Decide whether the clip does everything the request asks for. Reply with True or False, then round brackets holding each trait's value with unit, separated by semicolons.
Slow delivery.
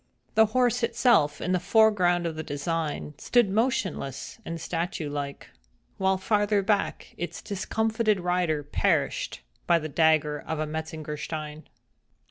True (125 wpm)